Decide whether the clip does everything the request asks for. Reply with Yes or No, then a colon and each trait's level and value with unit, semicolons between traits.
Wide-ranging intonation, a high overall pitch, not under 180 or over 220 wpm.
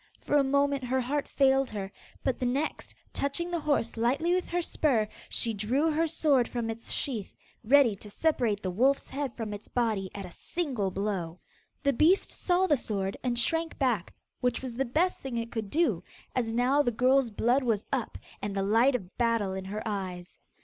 No: average, 4.9 semitones; high, 245 Hz; average, 200 wpm